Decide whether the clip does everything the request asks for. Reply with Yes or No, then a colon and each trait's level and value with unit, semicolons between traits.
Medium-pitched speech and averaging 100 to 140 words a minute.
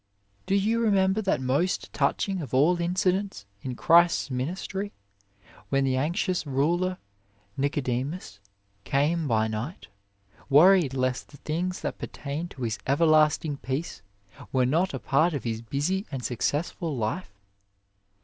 Yes: medium, 150 Hz; slow, 135 wpm